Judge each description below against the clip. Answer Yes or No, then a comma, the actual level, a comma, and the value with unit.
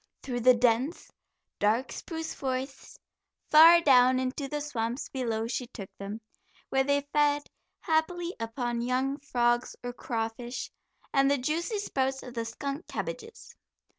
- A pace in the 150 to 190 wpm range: No, slow, 135 wpm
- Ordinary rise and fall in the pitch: Yes, average, 3.4 semitones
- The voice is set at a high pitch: Yes, very high, 260 Hz